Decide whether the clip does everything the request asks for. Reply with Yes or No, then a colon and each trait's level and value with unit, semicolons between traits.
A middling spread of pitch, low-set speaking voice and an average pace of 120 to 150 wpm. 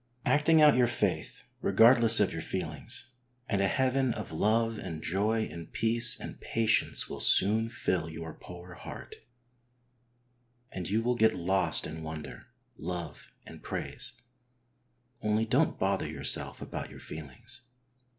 Yes: average, 4.9 semitones; low, 105 Hz; average, 140 wpm